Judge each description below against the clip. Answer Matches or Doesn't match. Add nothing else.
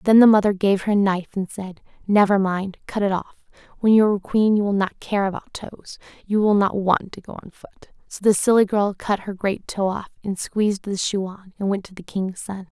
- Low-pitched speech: Doesn't match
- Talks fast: Matches